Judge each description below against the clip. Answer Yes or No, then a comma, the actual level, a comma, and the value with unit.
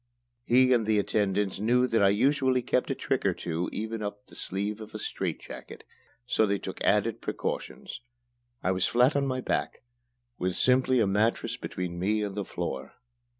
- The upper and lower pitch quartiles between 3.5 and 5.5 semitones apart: Yes, average, 4.0 semitones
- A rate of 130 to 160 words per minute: No, average, 185 wpm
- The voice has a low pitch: Yes, low, 110 Hz